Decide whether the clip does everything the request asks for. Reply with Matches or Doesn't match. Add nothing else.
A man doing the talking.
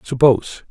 Matches